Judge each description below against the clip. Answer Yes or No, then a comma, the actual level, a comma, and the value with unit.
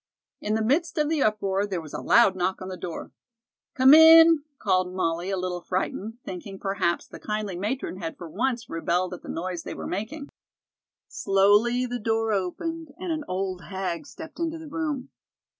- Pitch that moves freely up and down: Yes, wide, 7.1 semitones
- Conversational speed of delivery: Yes, average, 185 wpm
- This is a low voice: No, high, 205 Hz